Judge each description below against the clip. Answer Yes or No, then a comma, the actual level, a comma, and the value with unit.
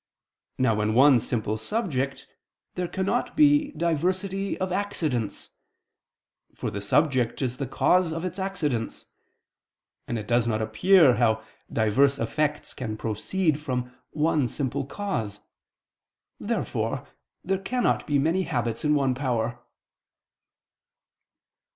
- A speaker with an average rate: No, slow, 120 wpm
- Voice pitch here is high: No, medium, 140 Hz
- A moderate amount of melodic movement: No, wide, 7.4 semitones